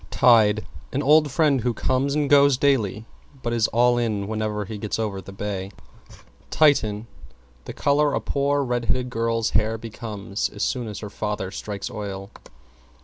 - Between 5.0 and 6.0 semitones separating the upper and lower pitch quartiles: No, average, 4.0 semitones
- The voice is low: Yes, low, 115 Hz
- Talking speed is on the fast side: No, average, 165 wpm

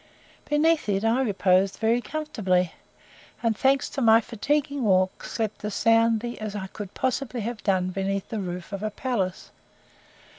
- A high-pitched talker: Yes, high, 220 Hz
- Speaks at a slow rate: No, average, 155 wpm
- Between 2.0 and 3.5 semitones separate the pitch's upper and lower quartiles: No, average, 3.9 semitones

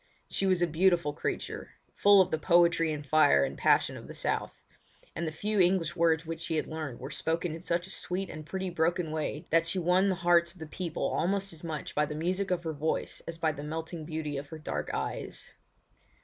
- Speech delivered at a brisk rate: Yes, fast, 225 wpm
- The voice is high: No, medium, 165 Hz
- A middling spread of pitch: No, narrow, 2.3 semitones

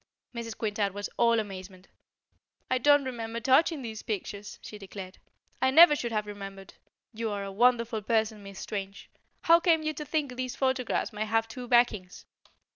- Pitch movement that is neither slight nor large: Yes, average, 3.9 semitones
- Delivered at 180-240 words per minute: No, average, 170 wpm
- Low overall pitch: No, high, 225 Hz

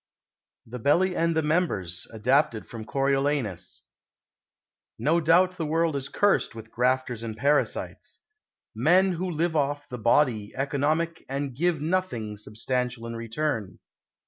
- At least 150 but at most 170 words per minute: No, slow, 135 wpm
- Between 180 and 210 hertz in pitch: No, medium, 140 Hz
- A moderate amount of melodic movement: No, wide, 5.8 semitones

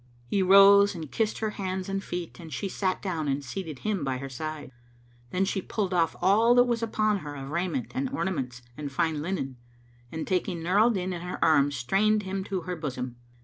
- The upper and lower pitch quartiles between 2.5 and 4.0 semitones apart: No, average, 4.8 semitones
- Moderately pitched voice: Yes, medium, 180 Hz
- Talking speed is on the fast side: Yes, fast, 210 wpm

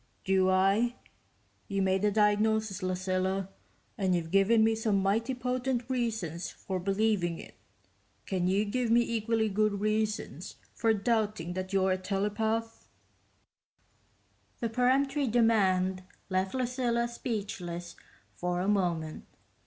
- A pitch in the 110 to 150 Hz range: No, high, 205 Hz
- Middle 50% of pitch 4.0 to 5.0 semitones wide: No, average, 3.4 semitones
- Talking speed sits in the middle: No, slow, 120 wpm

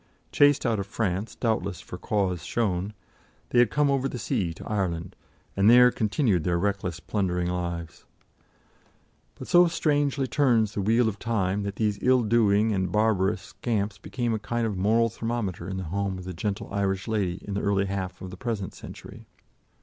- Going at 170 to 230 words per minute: Yes, average, 180 wpm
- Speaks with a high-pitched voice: No, low, 100 Hz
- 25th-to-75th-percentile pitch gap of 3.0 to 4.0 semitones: Yes, average, 3.5 semitones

